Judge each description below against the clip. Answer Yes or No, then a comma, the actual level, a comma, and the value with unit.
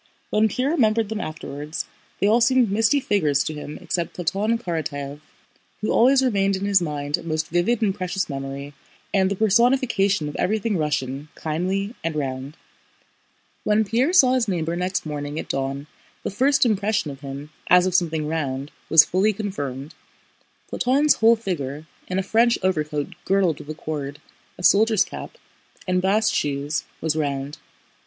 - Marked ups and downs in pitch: Yes, wide, 6.4 semitones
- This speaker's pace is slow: No, average, 160 wpm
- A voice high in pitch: No, medium, 180 Hz